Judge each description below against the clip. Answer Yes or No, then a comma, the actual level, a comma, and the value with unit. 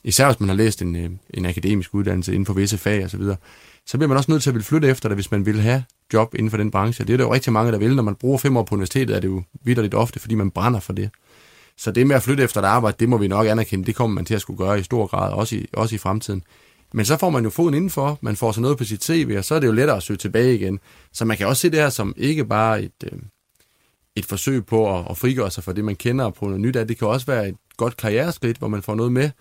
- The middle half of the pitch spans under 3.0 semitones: No, average, 3.9 semitones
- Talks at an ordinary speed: No, fast, 310 wpm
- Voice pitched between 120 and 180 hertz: No, low, 110 Hz